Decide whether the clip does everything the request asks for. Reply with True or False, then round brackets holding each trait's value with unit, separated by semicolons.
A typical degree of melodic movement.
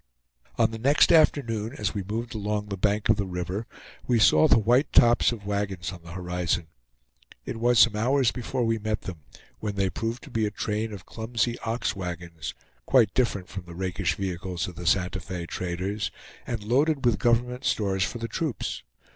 True (4.1 semitones)